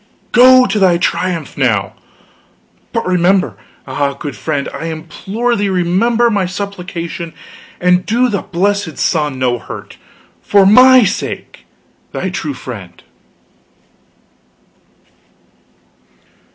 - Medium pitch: Yes, medium, 180 Hz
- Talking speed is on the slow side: Yes, slow, 105 wpm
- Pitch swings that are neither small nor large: Yes, average, 4.7 semitones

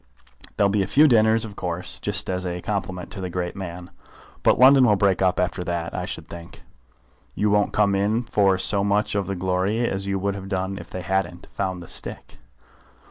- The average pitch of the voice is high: No, very low, 95 Hz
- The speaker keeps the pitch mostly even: Yes, narrow, 2.1 semitones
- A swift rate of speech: Yes, fast, 210 wpm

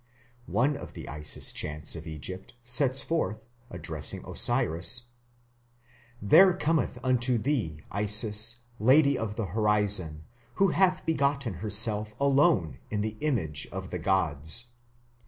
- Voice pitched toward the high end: No, low, 105 Hz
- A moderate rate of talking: No, slow, 120 wpm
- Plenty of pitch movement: Yes, wide, 6.9 semitones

